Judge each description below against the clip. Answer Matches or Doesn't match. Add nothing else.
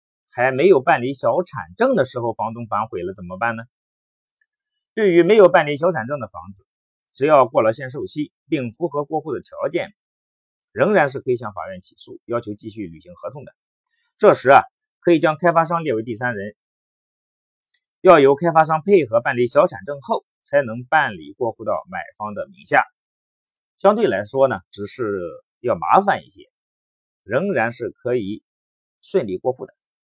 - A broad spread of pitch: Matches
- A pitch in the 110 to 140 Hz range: Matches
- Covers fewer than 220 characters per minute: Doesn't match